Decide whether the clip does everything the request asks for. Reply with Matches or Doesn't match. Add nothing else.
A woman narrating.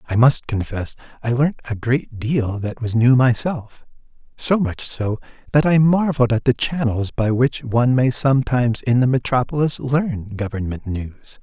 Doesn't match